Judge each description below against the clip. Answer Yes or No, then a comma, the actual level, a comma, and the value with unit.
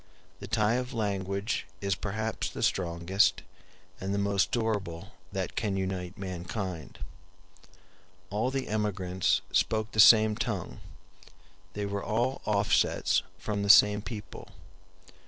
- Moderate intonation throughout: No, narrow, 2.3 semitones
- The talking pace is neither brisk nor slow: No, slow, 120 wpm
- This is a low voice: Yes, low, 100 Hz